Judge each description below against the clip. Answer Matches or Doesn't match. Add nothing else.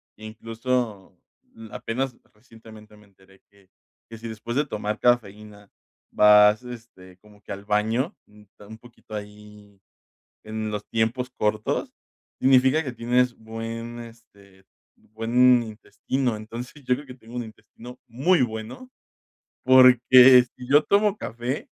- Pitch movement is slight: Doesn't match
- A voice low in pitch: Matches